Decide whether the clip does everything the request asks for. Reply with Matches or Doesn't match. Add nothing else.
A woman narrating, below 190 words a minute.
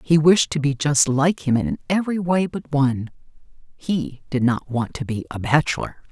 Doesn't match